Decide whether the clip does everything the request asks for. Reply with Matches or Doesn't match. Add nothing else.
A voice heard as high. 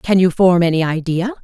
Doesn't match